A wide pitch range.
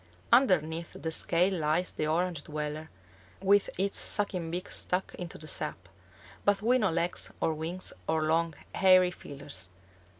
No: average, 2.9 semitones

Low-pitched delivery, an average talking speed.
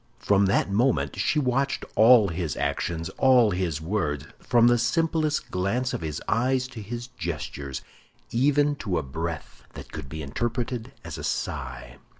Yes: low, 110 Hz; average, 155 wpm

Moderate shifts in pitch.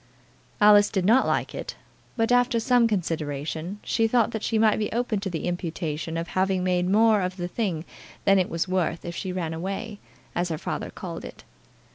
Yes: average, 4.2 semitones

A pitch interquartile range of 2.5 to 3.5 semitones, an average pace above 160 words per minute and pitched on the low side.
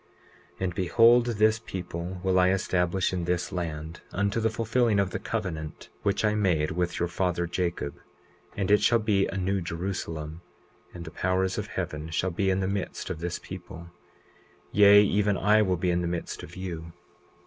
Yes: average, 2.8 semitones; average, 185 wpm; very low, 95 Hz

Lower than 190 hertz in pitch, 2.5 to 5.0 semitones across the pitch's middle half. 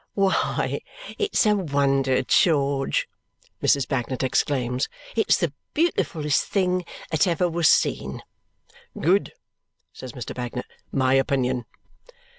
No: medium, 140 Hz; wide, 5.6 semitones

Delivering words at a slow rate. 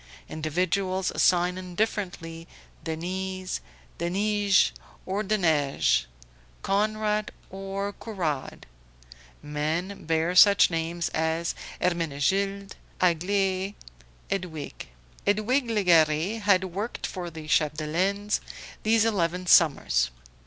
Yes: slow, 80 wpm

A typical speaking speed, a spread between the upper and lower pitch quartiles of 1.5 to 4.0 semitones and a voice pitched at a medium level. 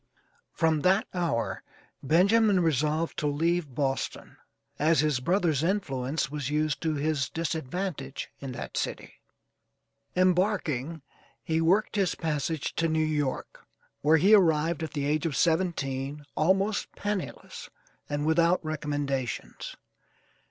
No: slow, 120 wpm; average, 3.3 semitones; medium, 155 Hz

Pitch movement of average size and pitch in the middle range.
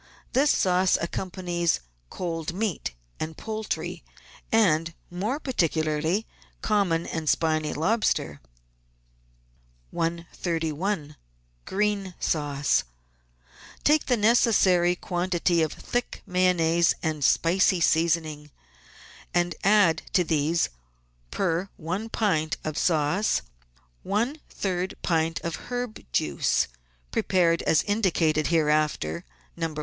Yes: average, 3.7 semitones; medium, 170 Hz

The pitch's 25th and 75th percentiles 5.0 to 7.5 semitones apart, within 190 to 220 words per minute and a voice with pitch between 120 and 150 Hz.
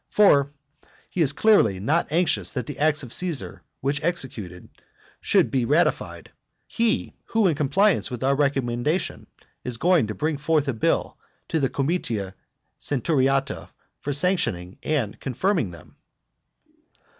No: wide, 5.4 semitones; slow, 135 wpm; medium, 140 Hz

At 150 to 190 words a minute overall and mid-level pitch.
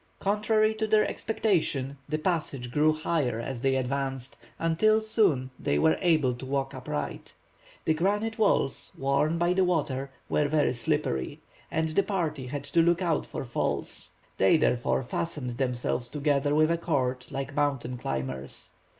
Yes: average, 155 wpm; medium, 145 Hz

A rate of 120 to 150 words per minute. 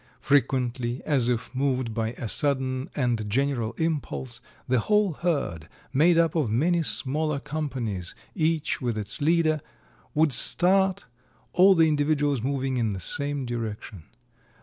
Yes: slow, 135 wpm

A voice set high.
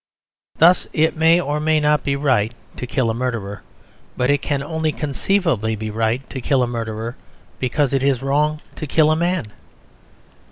No: medium, 140 Hz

